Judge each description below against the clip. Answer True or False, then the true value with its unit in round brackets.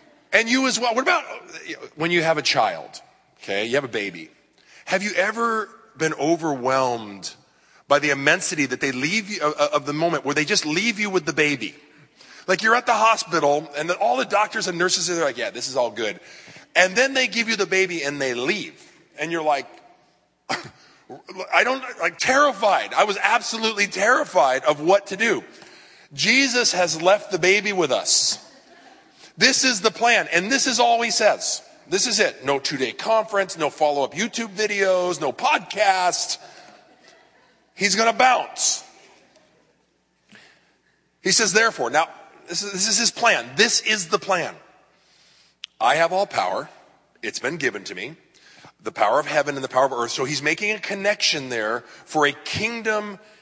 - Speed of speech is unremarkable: True (180 wpm)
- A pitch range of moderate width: False (6.6 semitones)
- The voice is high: True (200 Hz)